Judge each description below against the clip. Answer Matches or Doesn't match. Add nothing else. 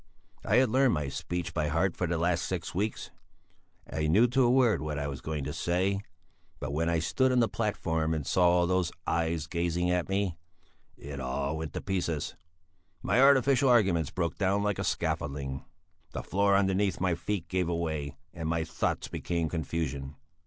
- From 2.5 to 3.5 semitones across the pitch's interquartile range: Doesn't match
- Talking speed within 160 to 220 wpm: Matches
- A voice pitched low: Matches